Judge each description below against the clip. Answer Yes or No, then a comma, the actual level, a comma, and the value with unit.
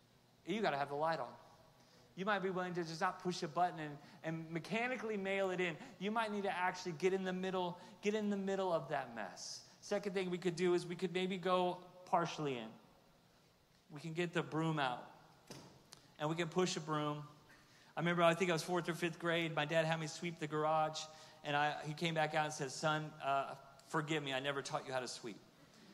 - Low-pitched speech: No, medium, 165 Hz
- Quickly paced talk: Yes, fast, 230 wpm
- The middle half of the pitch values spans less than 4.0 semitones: Yes, average, 3.1 semitones